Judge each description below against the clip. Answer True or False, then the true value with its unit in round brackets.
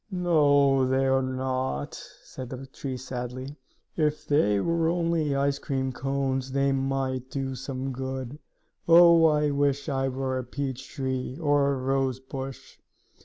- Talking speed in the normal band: True (145 wpm)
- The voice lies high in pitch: False (135 Hz)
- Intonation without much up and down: True (1.5 semitones)